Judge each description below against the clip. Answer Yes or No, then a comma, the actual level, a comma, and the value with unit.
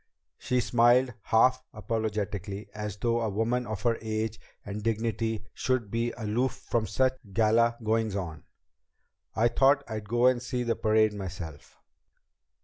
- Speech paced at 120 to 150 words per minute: Yes, average, 140 wpm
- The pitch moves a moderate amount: No, narrow, 2.1 semitones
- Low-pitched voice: Yes, low, 110 Hz